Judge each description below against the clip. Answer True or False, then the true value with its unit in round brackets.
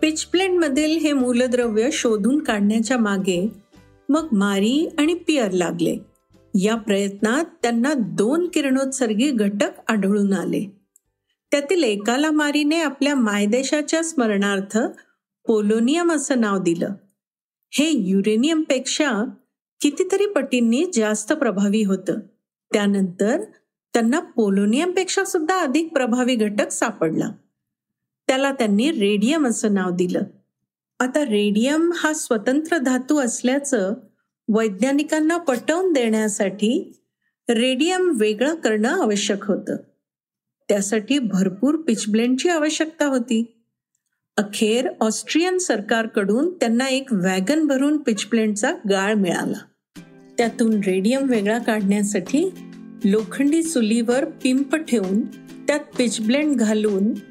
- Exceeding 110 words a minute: False (95 wpm)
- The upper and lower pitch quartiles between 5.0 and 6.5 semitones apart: True (5.6 semitones)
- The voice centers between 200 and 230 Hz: False (240 Hz)